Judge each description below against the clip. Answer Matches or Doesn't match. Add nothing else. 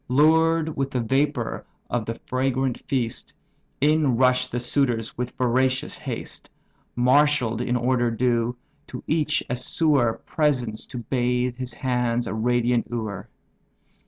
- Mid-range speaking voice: Doesn't match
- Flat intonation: Matches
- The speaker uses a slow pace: Matches